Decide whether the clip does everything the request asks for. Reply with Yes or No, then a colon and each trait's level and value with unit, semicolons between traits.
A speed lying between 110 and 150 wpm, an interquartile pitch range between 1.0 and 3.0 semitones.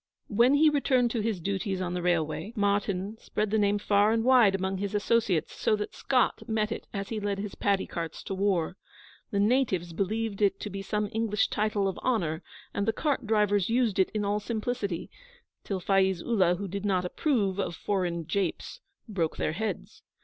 No: average, 195 wpm; narrow, 2.6 semitones